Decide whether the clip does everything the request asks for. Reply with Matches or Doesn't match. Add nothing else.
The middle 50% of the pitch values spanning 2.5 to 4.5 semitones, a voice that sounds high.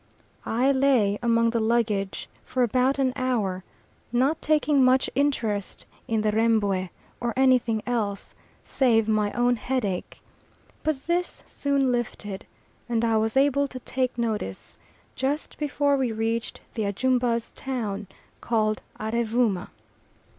Matches